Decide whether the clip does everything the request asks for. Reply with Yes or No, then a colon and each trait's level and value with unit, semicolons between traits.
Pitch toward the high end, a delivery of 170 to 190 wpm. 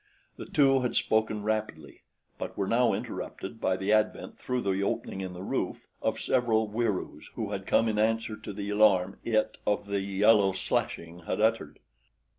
No: low, 105 Hz; average, 175 wpm